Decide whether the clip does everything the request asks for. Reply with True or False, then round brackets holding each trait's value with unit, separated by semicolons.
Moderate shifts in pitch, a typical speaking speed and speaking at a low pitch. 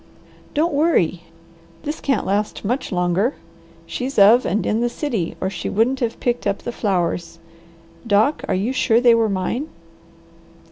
False (4.6 semitones; 155 wpm; 225 Hz)